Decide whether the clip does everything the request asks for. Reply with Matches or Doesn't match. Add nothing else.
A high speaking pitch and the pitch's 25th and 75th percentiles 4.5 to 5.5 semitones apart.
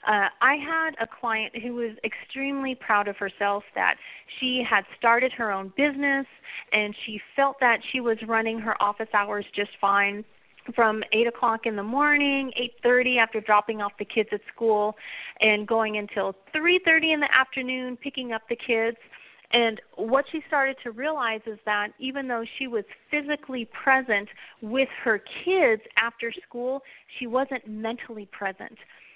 Doesn't match